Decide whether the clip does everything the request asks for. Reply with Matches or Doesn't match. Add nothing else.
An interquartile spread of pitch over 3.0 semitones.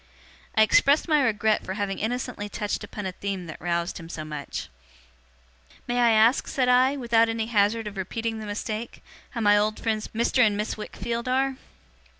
Doesn't match